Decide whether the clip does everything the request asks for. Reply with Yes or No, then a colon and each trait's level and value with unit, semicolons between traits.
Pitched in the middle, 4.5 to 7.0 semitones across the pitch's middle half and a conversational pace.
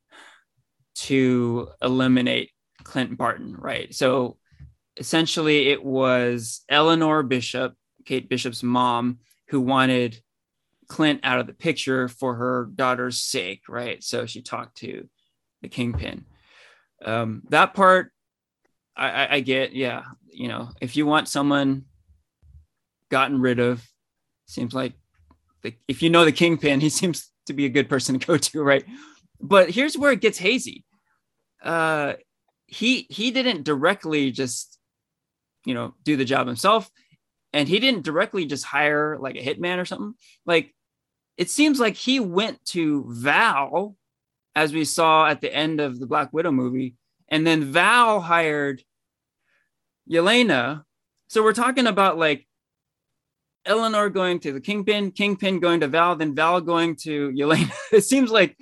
Yes: medium, 150 Hz; average, 5.3 semitones; average, 145 wpm